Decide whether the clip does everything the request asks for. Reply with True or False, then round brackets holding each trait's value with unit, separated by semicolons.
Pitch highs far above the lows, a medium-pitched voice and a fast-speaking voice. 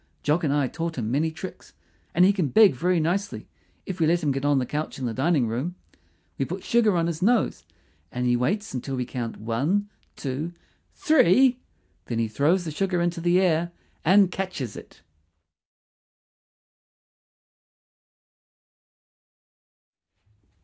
False (5.7 semitones; 165 Hz; 150 wpm)